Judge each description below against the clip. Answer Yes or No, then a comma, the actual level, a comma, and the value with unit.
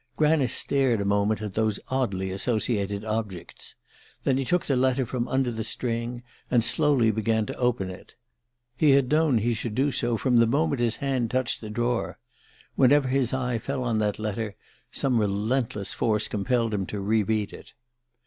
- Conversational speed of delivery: Yes, average, 180 wpm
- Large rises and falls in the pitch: No, average, 3.4 semitones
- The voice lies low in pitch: Yes, low, 115 Hz